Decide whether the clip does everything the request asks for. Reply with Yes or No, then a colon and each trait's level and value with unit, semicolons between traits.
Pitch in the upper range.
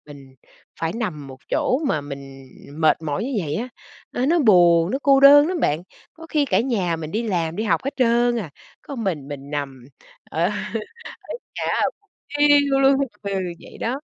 Yes: high, 195 Hz